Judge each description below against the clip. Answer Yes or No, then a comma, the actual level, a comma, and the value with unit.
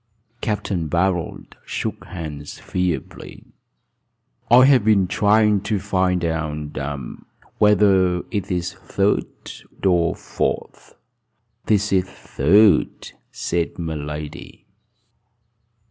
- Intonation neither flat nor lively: Yes, average, 3.7 semitones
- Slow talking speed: Yes, slow, 100 wpm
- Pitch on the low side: Yes, very low, 95 Hz